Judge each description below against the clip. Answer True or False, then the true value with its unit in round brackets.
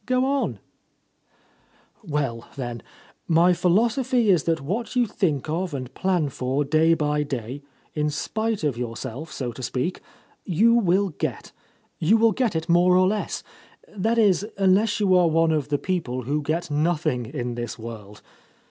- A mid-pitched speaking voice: True (165 Hz)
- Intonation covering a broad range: True (6.0 semitones)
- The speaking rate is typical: True (165 wpm)